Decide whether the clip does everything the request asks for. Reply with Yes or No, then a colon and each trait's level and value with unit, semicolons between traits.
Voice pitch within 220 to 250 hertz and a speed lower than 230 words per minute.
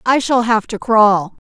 Yes: high, 225 Hz; average, 200 wpm